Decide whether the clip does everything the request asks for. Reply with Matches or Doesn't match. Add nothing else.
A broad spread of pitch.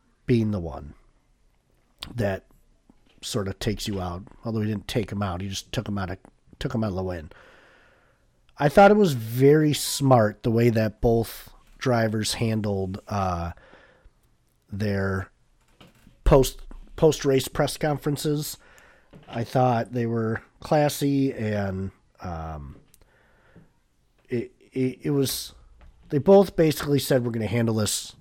Matches